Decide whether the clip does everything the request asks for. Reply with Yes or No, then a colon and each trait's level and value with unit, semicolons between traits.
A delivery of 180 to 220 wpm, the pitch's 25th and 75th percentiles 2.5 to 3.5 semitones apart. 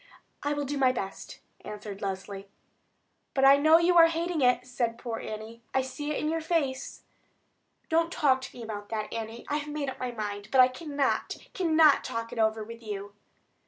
No: average, 195 wpm; average, 5.2 semitones